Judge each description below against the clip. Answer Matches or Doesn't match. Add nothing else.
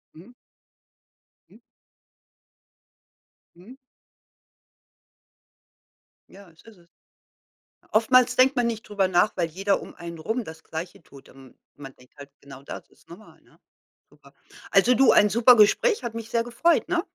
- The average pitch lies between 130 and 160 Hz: Doesn't match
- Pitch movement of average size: Doesn't match